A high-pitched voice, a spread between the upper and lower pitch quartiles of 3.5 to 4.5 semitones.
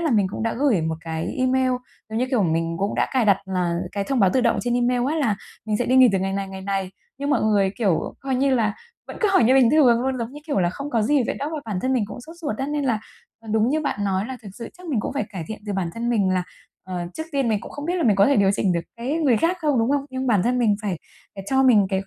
No: high, 230 Hz; average, 5.1 semitones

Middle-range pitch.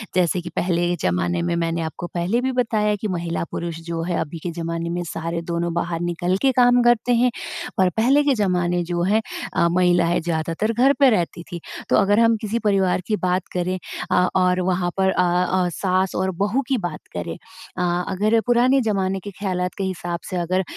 Yes: medium, 180 Hz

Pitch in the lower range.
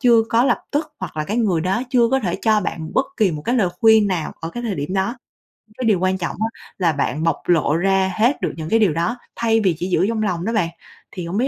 No: high, 195 Hz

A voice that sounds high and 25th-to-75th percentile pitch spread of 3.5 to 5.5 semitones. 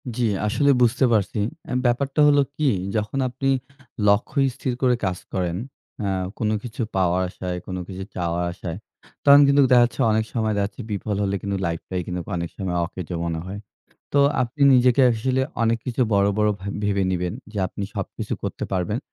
No: low, 105 Hz; average, 5.1 semitones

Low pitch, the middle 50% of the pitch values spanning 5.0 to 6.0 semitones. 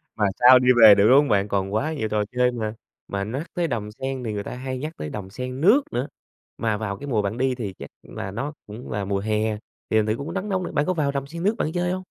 Yes: low, 125 Hz; average, 5.3 semitones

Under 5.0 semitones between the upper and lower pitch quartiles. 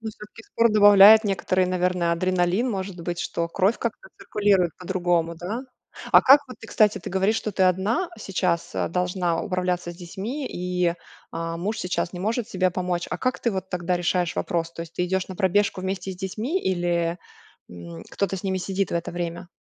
Yes: narrow, 2.6 semitones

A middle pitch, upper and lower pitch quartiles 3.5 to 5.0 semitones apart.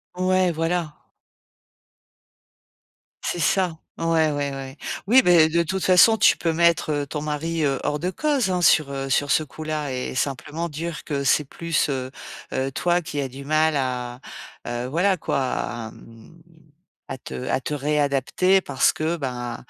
Yes: medium, 150 Hz; average, 3.8 semitones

